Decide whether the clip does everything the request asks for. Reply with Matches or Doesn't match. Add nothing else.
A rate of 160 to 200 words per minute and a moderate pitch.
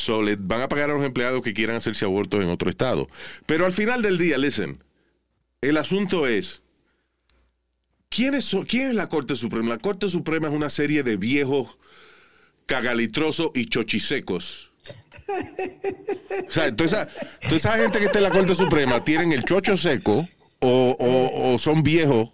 Matches